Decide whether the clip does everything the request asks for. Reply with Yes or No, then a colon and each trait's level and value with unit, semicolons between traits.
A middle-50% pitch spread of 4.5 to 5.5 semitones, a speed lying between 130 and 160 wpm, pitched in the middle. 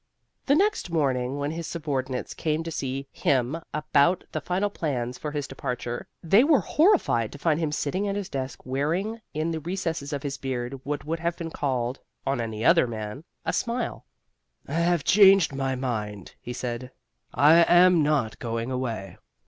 No: average, 4.8 semitones; average, 175 wpm; medium, 145 Hz